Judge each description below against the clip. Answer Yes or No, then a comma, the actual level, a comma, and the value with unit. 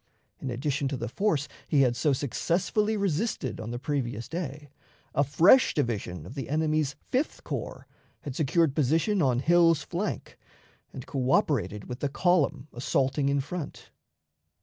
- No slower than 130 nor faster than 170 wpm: Yes, average, 150 wpm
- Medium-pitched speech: Yes, medium, 145 Hz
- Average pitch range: Yes, average, 4.3 semitones